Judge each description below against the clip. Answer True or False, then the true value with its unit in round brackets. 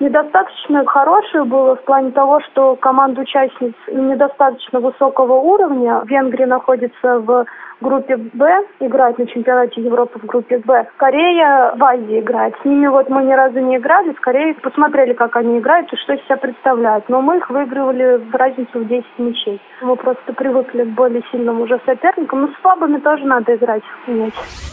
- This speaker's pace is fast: True (175 wpm)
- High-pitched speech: True (260 Hz)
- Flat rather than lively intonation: True (2.2 semitones)